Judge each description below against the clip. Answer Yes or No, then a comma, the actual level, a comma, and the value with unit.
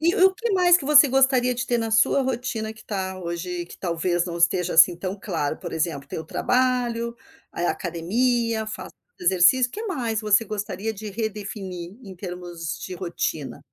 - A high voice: Yes, high, 210 Hz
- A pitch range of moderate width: No, wide, 5.8 semitones